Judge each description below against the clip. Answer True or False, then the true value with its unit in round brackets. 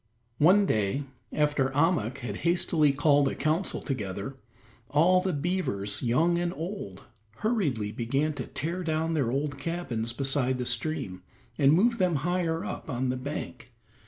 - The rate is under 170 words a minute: True (150 wpm)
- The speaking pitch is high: False (145 Hz)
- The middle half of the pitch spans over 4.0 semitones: True (5.2 semitones)